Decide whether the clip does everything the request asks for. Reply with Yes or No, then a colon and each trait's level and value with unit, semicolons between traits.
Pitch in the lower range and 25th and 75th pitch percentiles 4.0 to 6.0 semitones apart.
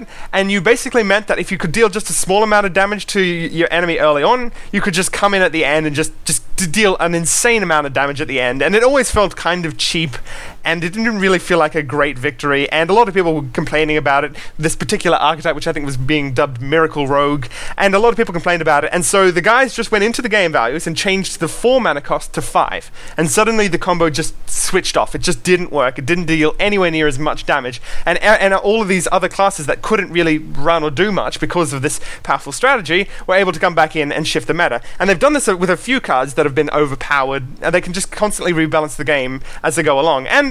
No: medium, 170 Hz; average, 4.4 semitones